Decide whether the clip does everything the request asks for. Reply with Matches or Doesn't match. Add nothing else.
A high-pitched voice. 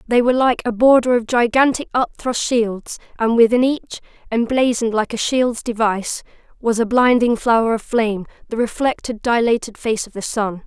Matches